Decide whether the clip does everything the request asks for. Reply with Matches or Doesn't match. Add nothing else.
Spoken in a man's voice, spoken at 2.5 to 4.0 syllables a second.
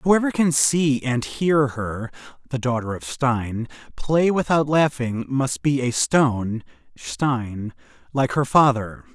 Matches